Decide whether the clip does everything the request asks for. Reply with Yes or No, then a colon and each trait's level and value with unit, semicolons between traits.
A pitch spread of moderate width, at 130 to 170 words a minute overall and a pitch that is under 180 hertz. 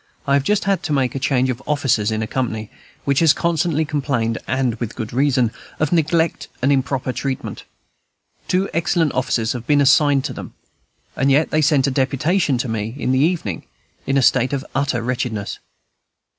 No: average, 3.2 semitones; average, 185 wpm; low, 135 Hz